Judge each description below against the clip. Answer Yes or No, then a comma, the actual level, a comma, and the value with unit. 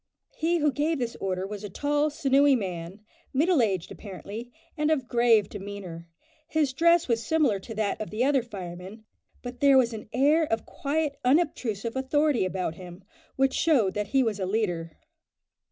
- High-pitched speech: Yes, high, 235 Hz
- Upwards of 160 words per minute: Yes, average, 170 wpm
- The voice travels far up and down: Yes, wide, 6.3 semitones